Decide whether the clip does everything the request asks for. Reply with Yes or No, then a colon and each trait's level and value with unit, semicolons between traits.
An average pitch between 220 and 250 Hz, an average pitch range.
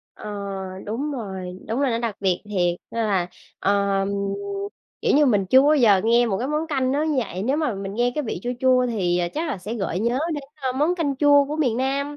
No: high, 240 Hz; wide, 6.0 semitones